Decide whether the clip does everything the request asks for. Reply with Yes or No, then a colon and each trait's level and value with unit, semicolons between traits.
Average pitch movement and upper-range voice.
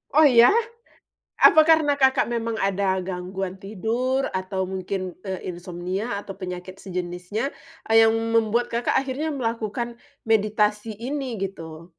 Yes: average, 4.2 semitones; high, 210 Hz